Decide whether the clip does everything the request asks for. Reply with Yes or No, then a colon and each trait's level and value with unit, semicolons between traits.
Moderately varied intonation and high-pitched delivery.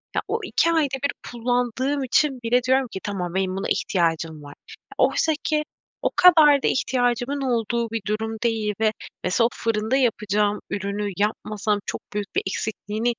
Yes: average, 4.0 semitones; high, 225 Hz